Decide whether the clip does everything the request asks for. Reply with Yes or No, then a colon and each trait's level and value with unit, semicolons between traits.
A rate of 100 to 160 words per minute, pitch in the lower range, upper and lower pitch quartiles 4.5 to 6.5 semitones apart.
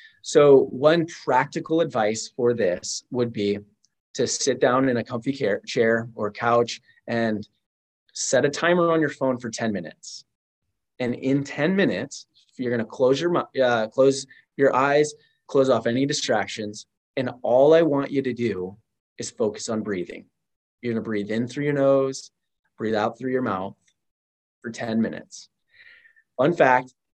No: average, 155 wpm; low, 125 Hz; average, 3.8 semitones